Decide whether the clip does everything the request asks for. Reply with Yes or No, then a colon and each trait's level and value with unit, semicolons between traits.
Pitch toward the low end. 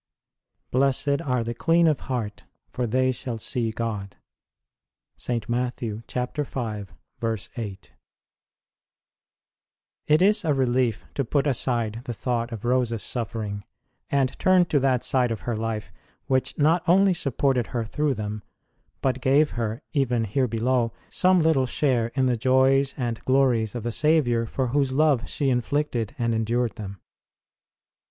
Yes: low, 125 Hz